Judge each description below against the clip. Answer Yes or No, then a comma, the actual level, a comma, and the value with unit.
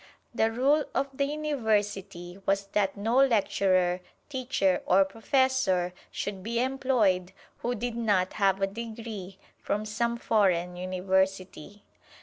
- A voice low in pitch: No, high, 205 Hz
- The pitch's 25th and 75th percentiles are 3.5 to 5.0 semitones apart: Yes, average, 4.0 semitones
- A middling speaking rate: No, slow, 125 wpm